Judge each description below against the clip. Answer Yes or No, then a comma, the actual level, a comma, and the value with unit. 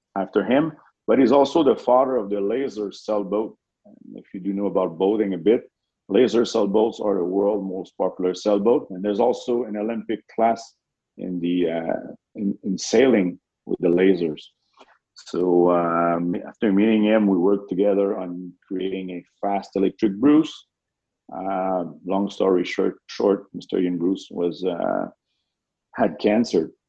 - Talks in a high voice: No, low, 100 Hz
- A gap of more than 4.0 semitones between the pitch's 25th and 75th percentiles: No, average, 2.9 semitones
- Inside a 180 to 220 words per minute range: No, average, 150 wpm